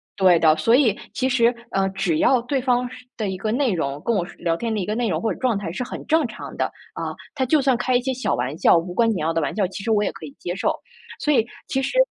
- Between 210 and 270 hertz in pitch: Yes, high, 220 Hz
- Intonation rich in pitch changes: Yes, wide, 5.9 semitones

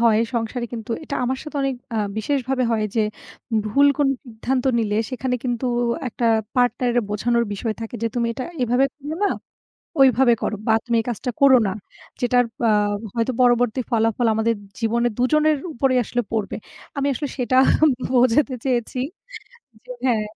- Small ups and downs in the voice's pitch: Yes, narrow, 2.3 semitones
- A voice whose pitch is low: No, high, 245 Hz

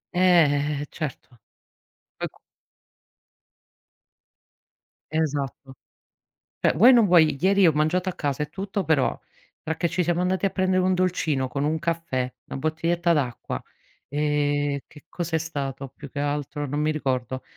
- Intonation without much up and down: No, average, 3.4 semitones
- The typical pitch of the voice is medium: Yes, medium, 155 Hz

